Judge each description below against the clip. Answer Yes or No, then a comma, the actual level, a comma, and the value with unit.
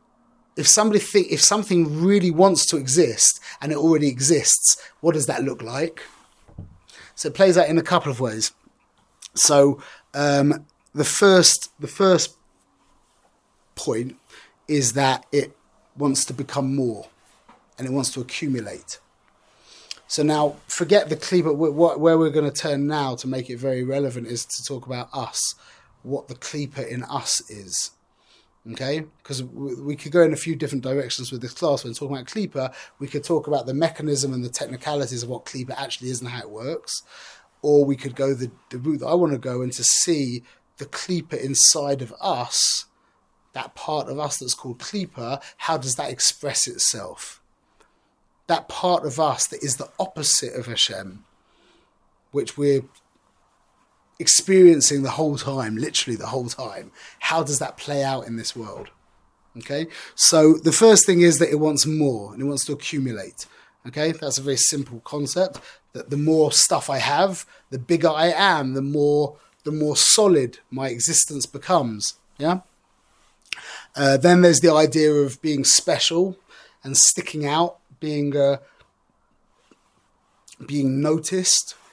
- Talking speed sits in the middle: Yes, average, 165 wpm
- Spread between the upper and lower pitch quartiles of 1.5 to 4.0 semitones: Yes, average, 3.6 semitones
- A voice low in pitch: No, medium, 145 Hz